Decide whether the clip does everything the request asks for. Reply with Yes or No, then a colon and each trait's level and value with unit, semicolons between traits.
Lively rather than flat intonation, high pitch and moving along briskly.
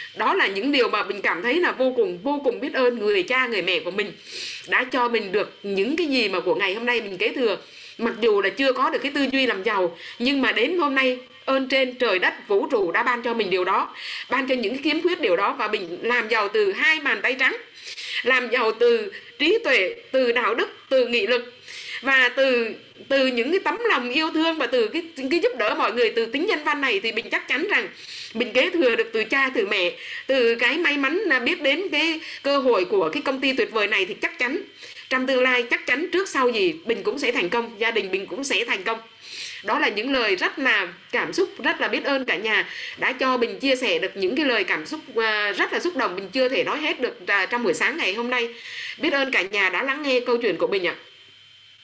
Yes: wide, 7.4 semitones; very high, 275 Hz; fast, 255 wpm